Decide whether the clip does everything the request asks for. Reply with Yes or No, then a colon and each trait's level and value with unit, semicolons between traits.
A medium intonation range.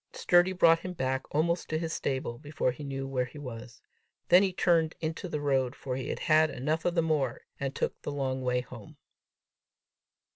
Yes: average, 4.0 semitones